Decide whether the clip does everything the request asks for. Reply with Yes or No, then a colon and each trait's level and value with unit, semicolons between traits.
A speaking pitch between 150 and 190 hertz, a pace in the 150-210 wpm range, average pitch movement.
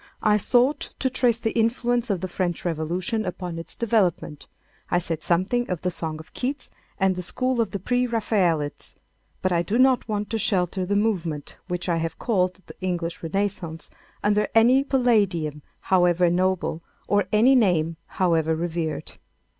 Yes: medium, 185 Hz; average, 165 wpm; average, 4.9 semitones